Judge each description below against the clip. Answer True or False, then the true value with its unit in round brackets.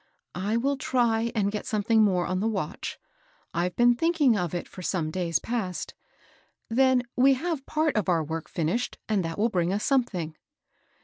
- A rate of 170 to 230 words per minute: True (190 wpm)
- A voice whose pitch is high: True (215 Hz)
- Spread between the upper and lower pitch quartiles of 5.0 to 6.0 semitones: True (5.6 semitones)